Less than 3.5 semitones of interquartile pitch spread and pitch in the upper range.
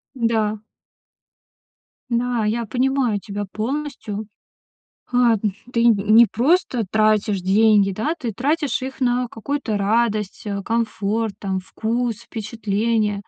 Yes: average, 2.7 semitones; high, 225 Hz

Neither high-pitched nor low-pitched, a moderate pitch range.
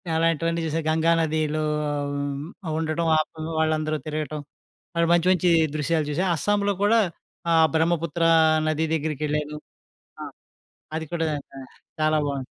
No: medium, 160 Hz; narrow, 1.5 semitones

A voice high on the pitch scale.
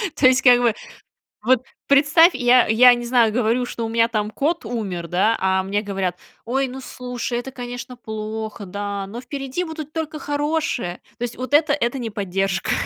Yes: high, 240 Hz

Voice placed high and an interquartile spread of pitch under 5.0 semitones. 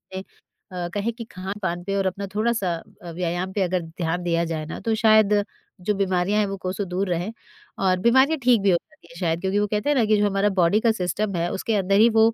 Yes: high, 195 Hz; average, 3.1 semitones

